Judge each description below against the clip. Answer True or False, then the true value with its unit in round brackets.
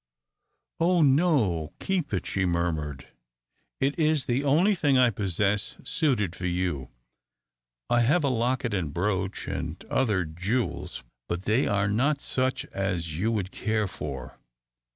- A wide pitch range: True (6.9 semitones)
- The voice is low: True (105 Hz)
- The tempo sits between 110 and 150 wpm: True (140 wpm)